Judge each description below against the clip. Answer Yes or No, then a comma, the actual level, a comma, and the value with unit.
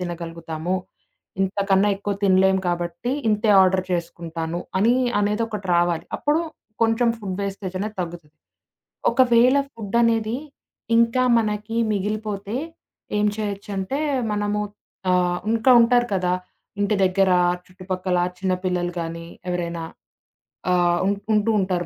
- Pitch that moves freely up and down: No, average, 3.2 semitones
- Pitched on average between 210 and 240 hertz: No, high, 195 Hz